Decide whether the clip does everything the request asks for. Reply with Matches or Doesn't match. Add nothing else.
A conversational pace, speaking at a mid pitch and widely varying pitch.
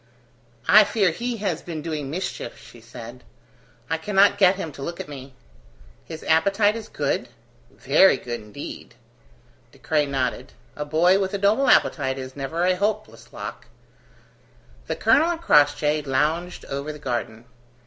Matches